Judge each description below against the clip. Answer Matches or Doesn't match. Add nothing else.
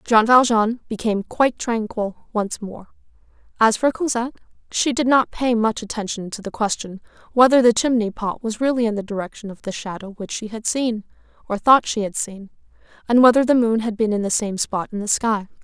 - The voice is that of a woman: Matches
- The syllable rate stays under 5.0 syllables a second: Doesn't match